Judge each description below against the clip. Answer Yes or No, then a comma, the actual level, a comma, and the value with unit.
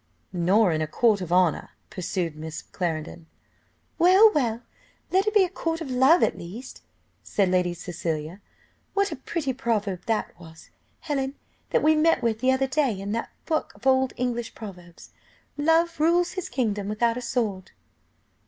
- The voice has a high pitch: Yes, high, 230 Hz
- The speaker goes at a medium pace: Yes, average, 165 wpm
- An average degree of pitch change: No, wide, 8.3 semitones